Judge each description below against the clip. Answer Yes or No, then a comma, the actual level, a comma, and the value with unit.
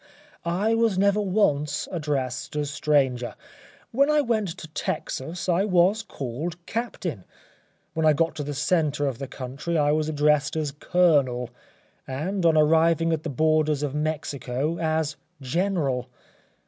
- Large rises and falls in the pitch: No, average, 3.6 semitones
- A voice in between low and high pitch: Yes, medium, 155 Hz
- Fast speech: No, average, 150 wpm